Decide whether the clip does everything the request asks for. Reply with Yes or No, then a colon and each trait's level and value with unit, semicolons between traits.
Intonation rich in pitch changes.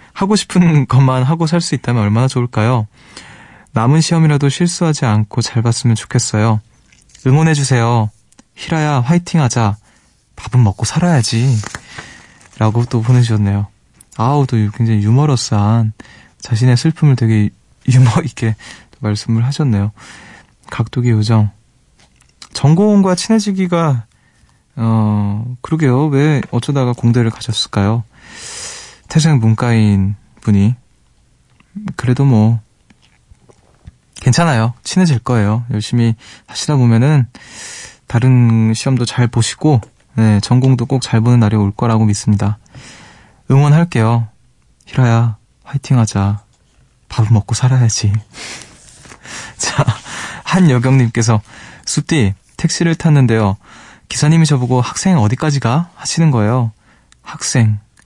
No: average, 4.0 semitones